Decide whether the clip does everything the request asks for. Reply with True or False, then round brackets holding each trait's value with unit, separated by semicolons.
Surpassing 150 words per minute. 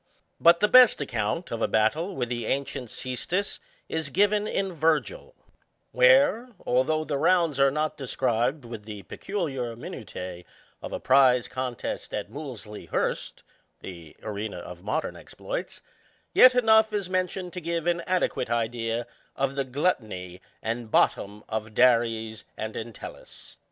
False (145 wpm)